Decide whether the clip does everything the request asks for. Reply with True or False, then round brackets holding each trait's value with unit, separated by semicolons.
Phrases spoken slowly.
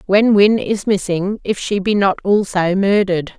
False (175 wpm)